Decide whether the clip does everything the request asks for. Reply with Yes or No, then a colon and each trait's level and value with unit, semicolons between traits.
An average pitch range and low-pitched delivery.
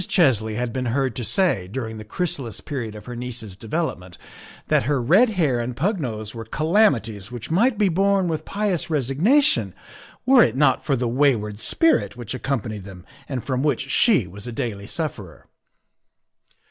No: wide, 7.0 semitones; low, 130 Hz